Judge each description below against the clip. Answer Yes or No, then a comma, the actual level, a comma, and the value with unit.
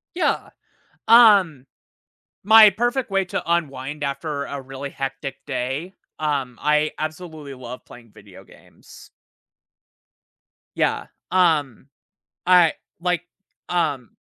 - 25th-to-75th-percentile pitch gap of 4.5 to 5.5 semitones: Yes, average, 4.9 semitones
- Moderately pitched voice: Yes, medium, 150 Hz